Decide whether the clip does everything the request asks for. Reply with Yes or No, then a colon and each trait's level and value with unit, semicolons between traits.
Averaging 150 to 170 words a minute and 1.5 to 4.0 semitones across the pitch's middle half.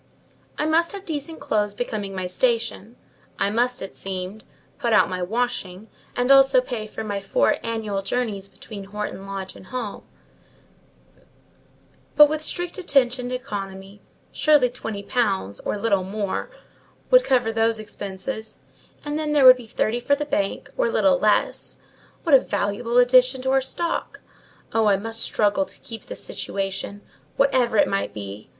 No: average, 160 wpm; average, 4.5 semitones